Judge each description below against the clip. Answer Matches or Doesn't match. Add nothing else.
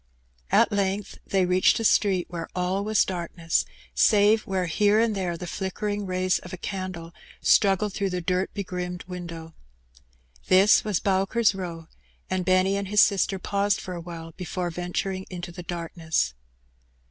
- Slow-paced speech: Doesn't match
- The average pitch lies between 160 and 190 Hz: Matches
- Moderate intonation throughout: Doesn't match